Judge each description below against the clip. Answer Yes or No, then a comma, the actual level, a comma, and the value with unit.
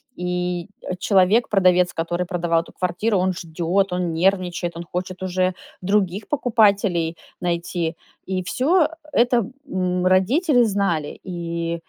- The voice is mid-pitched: Yes, medium, 180 Hz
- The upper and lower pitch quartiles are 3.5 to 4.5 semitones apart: No, narrow, 2.4 semitones